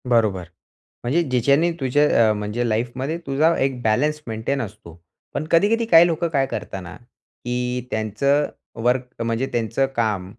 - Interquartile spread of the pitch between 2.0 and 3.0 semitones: No, average, 4.3 semitones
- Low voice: Yes, low, 125 Hz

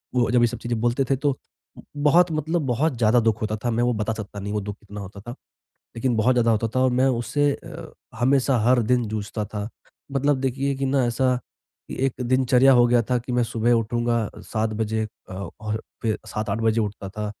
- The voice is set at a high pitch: No, low, 120 Hz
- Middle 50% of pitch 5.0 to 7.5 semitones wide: No, average, 3.1 semitones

